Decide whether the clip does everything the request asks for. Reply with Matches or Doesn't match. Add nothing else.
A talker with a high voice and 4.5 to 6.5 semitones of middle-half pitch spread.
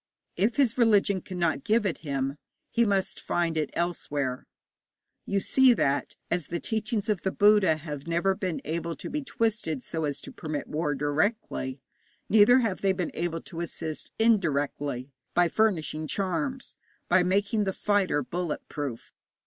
Doesn't match